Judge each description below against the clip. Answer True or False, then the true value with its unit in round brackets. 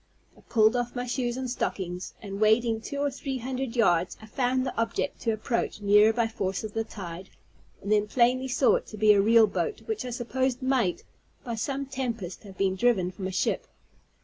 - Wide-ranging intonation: False (3.6 semitones)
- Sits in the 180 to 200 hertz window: False (225 Hz)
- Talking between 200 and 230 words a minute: True (205 wpm)